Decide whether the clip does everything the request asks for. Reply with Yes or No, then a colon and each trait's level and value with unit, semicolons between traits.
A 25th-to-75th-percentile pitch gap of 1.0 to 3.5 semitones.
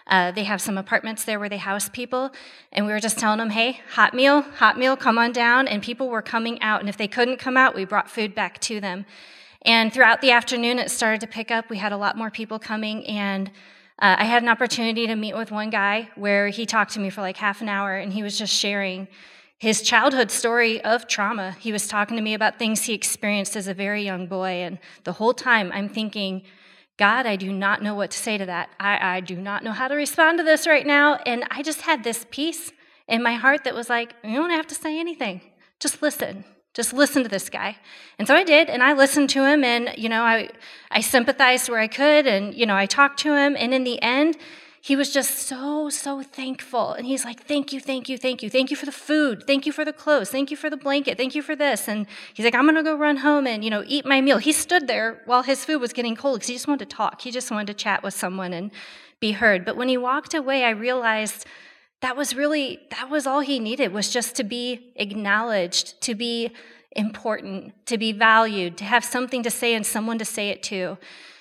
No: average, 4.5 semitones